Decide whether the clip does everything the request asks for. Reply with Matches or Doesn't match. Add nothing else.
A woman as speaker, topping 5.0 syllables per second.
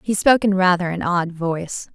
Matches